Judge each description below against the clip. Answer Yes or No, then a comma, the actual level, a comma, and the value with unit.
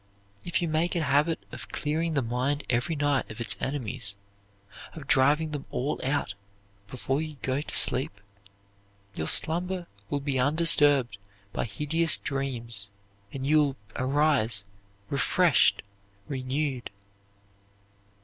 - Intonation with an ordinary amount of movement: Yes, average, 3.4 semitones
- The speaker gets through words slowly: Yes, slow, 125 wpm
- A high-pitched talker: No, medium, 140 Hz